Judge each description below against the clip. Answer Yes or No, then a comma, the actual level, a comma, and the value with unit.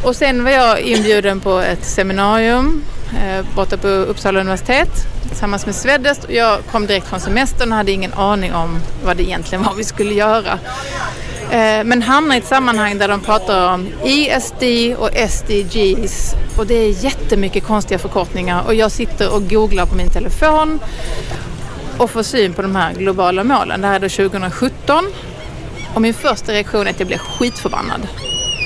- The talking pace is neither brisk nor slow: Yes, average, 175 wpm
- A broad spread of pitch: No, average, 3.5 semitones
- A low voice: No, high, 210 Hz